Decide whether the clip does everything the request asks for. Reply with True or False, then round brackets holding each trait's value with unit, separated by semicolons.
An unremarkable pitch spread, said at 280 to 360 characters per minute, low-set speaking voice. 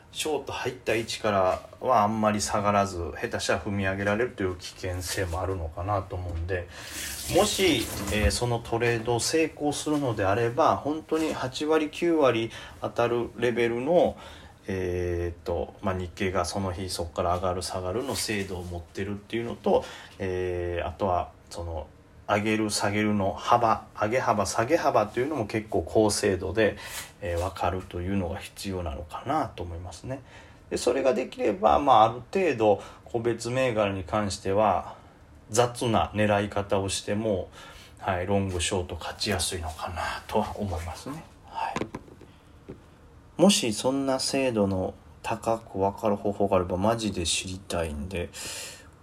True (3.9 semitones; 315 characters per minute; 100 Hz)